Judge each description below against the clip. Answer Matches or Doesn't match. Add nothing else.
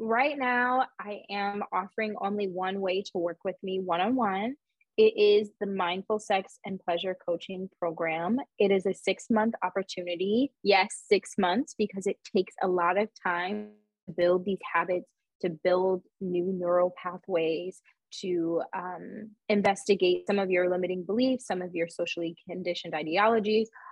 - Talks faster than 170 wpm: Doesn't match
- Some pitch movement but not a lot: Matches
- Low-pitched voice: Doesn't match